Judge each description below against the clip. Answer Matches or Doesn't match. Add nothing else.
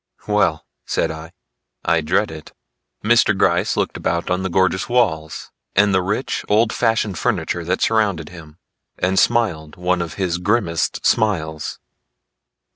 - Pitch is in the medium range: Doesn't match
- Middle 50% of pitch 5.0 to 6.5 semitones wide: Doesn't match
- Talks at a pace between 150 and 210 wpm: Doesn't match